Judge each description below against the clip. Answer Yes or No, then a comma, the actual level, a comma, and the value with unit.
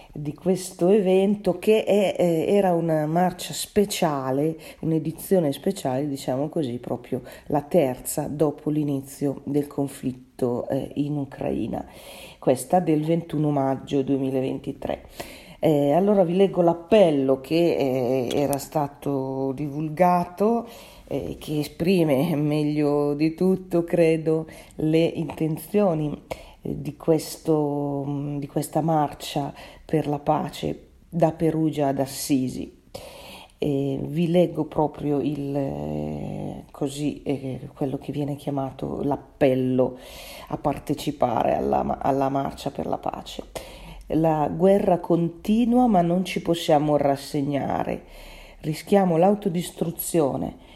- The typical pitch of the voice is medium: Yes, medium, 150 Hz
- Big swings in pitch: No, average, 3.3 semitones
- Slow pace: Yes, slow, 105 wpm